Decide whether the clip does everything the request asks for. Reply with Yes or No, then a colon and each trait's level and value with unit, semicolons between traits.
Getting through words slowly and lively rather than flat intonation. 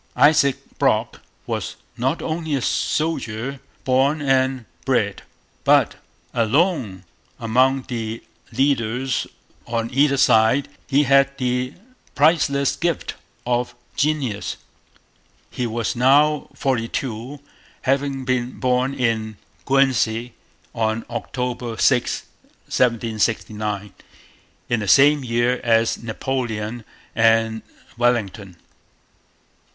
No: slow, 95 wpm; average, 3.3 semitones